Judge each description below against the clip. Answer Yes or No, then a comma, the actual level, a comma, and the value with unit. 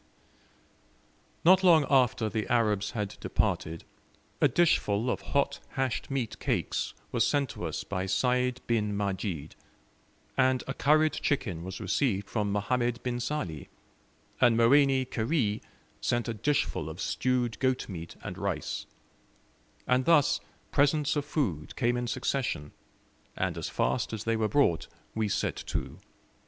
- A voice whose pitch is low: Yes, low, 120 Hz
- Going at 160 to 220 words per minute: No, average, 140 wpm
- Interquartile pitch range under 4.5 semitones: No, average, 4.9 semitones